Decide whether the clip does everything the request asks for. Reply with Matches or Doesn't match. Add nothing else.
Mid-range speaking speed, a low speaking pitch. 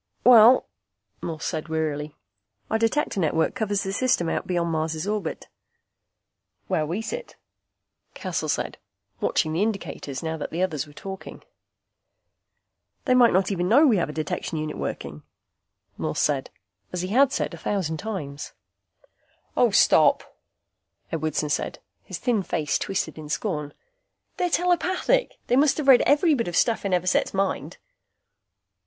Doesn't match